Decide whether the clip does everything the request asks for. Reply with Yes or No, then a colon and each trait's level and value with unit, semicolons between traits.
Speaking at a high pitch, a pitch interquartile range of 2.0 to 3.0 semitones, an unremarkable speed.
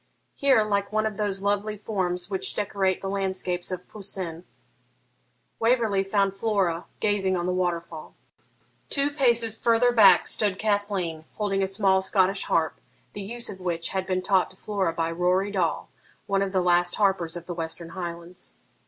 Yes: high, 195 Hz; narrow, 2.5 semitones; average, 165 wpm